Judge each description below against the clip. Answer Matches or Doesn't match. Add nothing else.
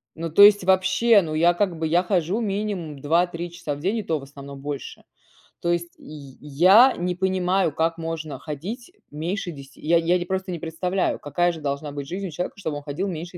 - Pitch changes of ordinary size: Matches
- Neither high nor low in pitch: Matches